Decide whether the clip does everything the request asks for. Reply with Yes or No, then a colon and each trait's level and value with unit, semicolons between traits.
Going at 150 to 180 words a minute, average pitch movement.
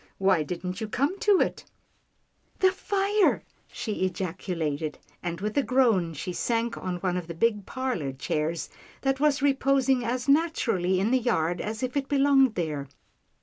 No: average, 175 wpm; wide, 7.3 semitones